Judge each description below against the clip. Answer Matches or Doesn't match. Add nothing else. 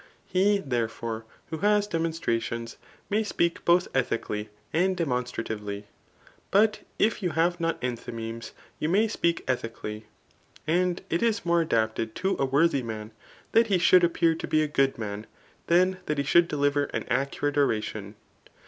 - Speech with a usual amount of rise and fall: Doesn't match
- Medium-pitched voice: Matches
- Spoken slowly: Doesn't match